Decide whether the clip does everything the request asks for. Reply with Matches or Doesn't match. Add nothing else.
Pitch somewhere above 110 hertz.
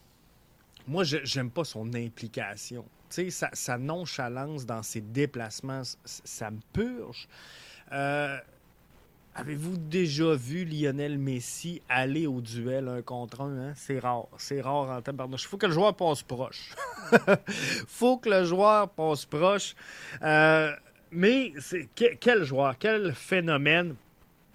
Matches